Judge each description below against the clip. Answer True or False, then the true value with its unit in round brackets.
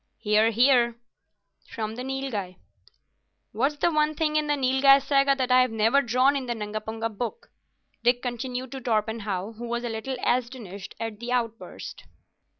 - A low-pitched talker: False (245 Hz)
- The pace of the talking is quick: False (155 wpm)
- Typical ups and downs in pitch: True (3.3 semitones)